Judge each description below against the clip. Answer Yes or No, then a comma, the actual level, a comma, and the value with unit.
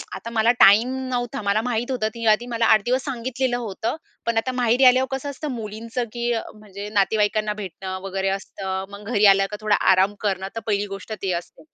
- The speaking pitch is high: Yes, high, 220 Hz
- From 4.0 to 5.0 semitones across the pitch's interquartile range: No, average, 3.3 semitones